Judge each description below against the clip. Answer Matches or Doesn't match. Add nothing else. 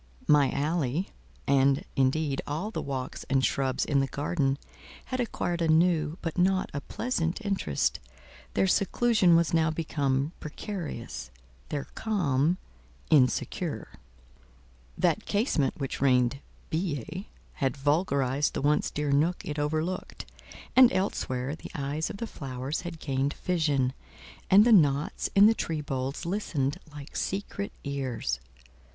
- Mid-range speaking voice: Matches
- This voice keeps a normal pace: Doesn't match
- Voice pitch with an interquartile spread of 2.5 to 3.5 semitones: Doesn't match